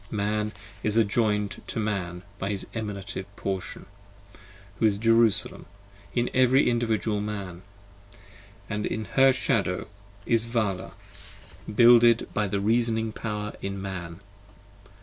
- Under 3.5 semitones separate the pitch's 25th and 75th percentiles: Yes, narrow, 2.6 semitones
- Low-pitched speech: Yes, low, 105 Hz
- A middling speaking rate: No, slow, 115 wpm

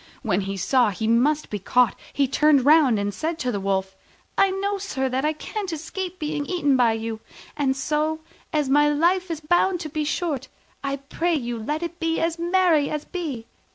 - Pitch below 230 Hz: No, very high, 295 Hz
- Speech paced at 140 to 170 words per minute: No, fast, 205 wpm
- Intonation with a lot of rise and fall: No, average, 5.0 semitones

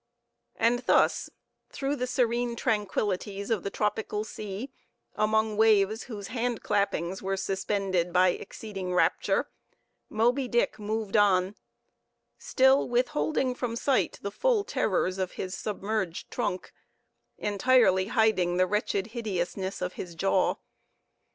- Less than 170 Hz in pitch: No, high, 210 Hz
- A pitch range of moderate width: Yes, average, 3.7 semitones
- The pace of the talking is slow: Yes, slow, 120 wpm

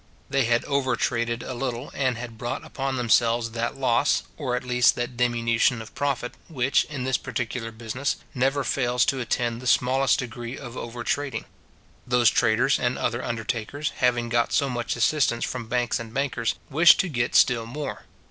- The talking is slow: No, average, 175 wpm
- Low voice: Yes, low, 120 Hz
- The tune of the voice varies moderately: No, narrow, 2.1 semitones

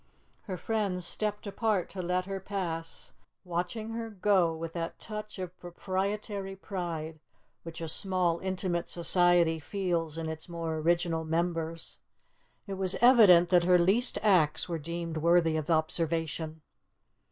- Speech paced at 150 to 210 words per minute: No, average, 140 wpm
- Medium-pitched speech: Yes, medium, 175 Hz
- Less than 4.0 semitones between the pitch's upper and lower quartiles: Yes, average, 2.7 semitones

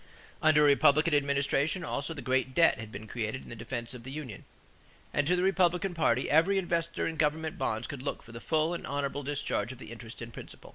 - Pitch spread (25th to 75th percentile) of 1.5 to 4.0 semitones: No, average, 4.8 semitones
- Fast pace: Yes, fast, 225 wpm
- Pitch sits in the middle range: Yes, medium, 145 Hz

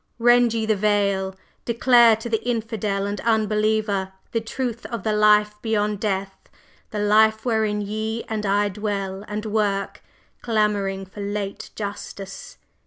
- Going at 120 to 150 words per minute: Yes, average, 140 wpm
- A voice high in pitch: Yes, high, 210 Hz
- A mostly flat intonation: Yes, narrow, 1.7 semitones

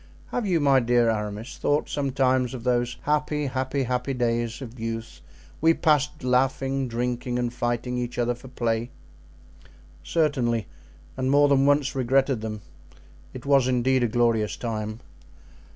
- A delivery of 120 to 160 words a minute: Yes, average, 145 wpm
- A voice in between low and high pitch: No, low, 125 Hz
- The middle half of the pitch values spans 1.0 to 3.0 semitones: Yes, narrow, 2.4 semitones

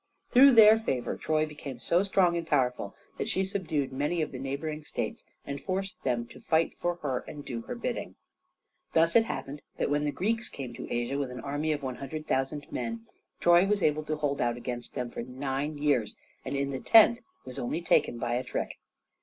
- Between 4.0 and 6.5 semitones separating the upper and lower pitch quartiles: Yes, average, 4.7 semitones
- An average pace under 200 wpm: No, fast, 205 wpm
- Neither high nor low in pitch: Yes, medium, 145 Hz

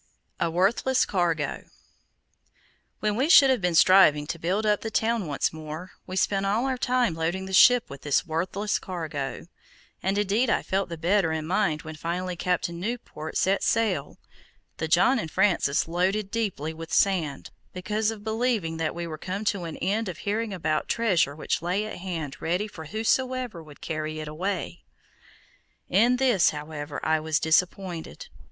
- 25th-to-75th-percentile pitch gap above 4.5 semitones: Yes, average, 4.9 semitones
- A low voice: No, medium, 180 Hz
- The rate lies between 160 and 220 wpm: Yes, average, 175 wpm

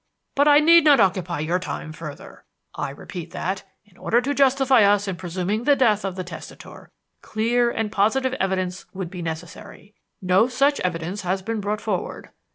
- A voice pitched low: No, high, 200 Hz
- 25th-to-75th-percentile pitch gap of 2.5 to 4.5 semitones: No, average, 5.1 semitones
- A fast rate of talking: No, average, 180 wpm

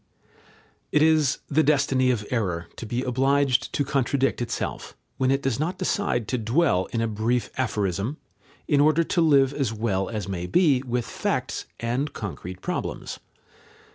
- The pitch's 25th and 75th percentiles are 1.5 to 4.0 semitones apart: No, average, 4.4 semitones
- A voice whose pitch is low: Yes, low, 125 Hz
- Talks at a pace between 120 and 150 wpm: No, average, 160 wpm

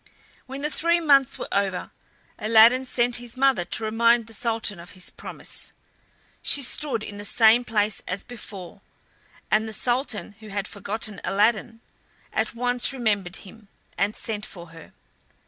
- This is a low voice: No, high, 220 Hz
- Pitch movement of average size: Yes, average, 3.2 semitones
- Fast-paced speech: No, average, 155 wpm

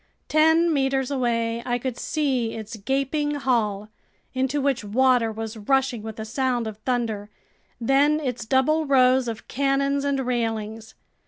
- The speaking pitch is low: No, very high, 255 Hz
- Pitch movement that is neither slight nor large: Yes, average, 3.4 semitones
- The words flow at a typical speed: Yes, average, 145 wpm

